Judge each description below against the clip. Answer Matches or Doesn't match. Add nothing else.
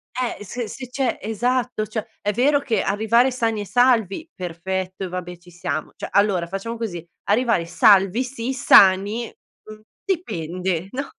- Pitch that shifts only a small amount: Doesn't match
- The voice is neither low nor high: Doesn't match